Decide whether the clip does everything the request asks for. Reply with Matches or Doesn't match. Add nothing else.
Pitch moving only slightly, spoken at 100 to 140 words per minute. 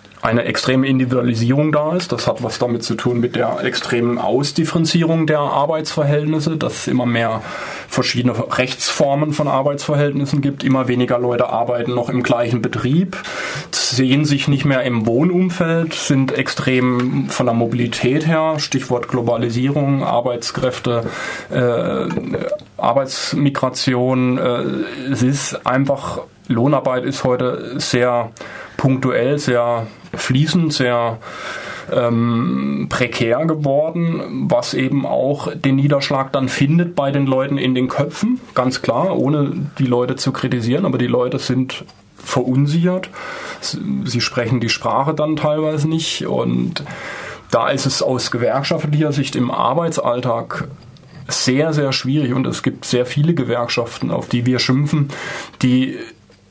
Doesn't match